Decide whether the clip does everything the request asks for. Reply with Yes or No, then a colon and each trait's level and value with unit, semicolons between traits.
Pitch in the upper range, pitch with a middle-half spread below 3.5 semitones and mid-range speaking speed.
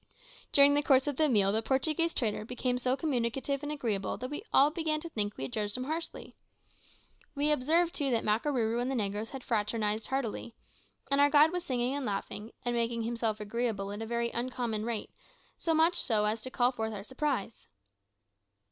No: high, 245 Hz; average, 4.5 semitones; average, 195 wpm